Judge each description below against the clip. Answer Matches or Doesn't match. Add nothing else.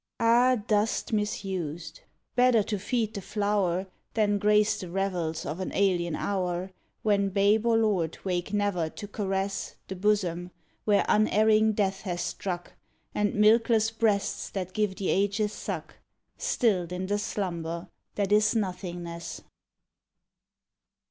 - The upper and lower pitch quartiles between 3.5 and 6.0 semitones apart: Doesn't match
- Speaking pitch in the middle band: Doesn't match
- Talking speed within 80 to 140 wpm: Matches